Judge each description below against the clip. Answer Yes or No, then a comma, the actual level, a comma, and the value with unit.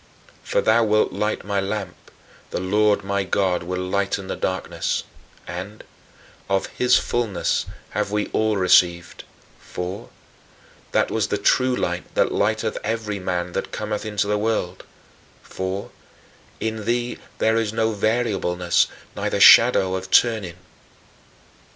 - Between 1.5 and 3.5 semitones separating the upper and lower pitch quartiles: Yes, average, 2.8 semitones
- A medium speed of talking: No, slow, 130 wpm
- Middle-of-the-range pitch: No, low, 100 Hz